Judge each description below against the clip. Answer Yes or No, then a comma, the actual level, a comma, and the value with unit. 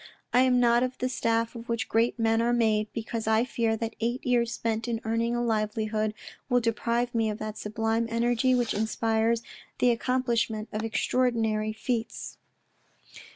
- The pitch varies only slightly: Yes, narrow, 1.4 semitones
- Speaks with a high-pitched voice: Yes, high, 230 Hz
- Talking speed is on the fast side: No, average, 170 wpm